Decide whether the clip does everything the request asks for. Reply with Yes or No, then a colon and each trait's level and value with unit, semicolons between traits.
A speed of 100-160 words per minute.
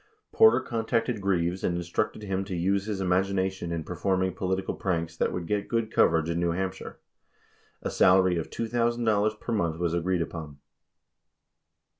No: average, 170 wpm